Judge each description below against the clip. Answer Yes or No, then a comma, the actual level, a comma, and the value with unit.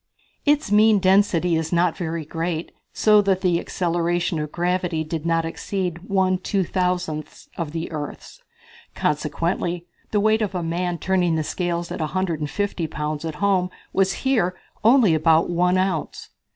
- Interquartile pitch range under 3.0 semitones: Yes, narrow, 2.6 semitones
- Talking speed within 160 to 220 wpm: No, average, 150 wpm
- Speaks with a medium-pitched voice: Yes, medium, 175 Hz